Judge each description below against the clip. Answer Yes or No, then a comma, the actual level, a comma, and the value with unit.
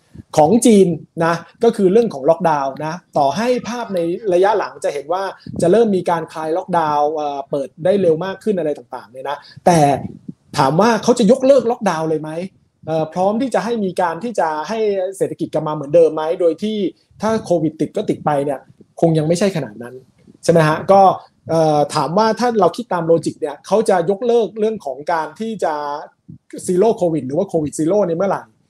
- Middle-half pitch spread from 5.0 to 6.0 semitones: Yes, average, 5.3 semitones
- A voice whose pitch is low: No, medium, 170 Hz